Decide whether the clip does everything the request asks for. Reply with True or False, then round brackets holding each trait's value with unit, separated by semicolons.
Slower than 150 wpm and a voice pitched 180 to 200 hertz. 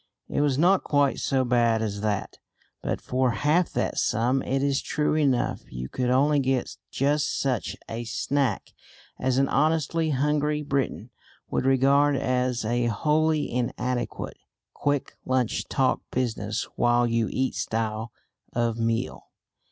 False (140 wpm; 130 Hz)